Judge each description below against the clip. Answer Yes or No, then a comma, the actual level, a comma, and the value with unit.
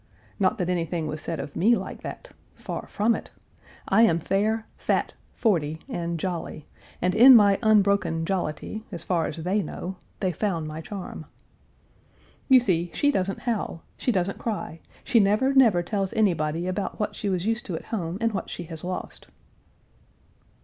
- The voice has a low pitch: No, high, 190 Hz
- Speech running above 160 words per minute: Yes, average, 170 wpm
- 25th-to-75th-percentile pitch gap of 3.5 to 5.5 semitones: Yes, average, 4.3 semitones